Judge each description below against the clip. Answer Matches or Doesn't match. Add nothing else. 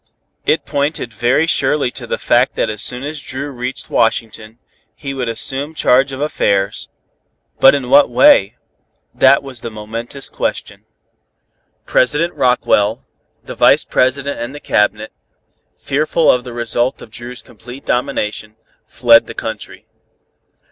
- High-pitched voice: Doesn't match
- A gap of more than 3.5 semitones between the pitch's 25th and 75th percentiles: Doesn't match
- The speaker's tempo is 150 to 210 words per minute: Doesn't match